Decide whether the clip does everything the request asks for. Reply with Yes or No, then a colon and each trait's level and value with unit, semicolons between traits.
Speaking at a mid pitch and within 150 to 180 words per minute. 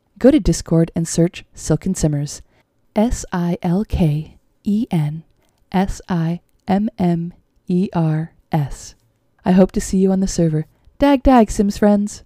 Yes: medium, 175 Hz; average, 155 wpm